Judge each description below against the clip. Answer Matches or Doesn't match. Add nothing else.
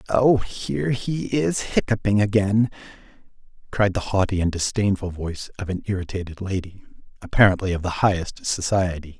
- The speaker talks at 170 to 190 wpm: Doesn't match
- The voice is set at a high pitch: Doesn't match